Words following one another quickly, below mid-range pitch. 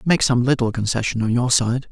Yes: fast, 220 wpm; low, 120 Hz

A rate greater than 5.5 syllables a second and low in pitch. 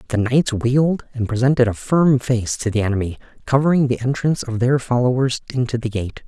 Yes: 5.8 syllables/s; low, 125 Hz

